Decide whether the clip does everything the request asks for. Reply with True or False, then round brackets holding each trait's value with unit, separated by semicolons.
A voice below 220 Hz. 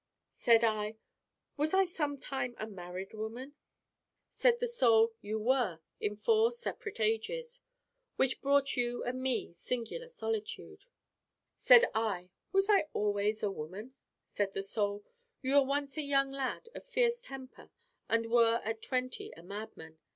False (245 Hz)